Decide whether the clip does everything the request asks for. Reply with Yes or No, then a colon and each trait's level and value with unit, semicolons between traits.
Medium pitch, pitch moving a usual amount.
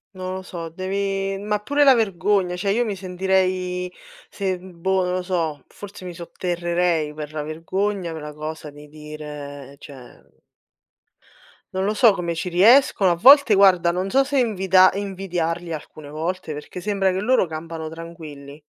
Yes: medium, 180 Hz; average, 3.3 semitones